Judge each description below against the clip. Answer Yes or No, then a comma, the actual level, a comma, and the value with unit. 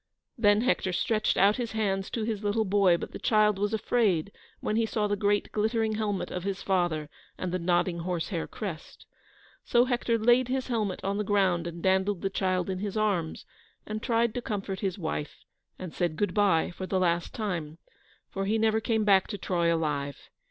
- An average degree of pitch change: Yes, average, 3.2 semitones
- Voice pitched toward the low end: No, high, 200 Hz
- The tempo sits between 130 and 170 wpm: No, average, 195 wpm